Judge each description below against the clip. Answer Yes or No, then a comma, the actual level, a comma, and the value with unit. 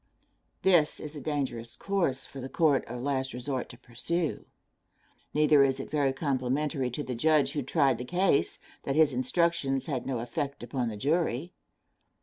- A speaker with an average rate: Yes, average, 165 wpm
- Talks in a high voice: No, medium, 140 Hz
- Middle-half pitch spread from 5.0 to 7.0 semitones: No, average, 3.1 semitones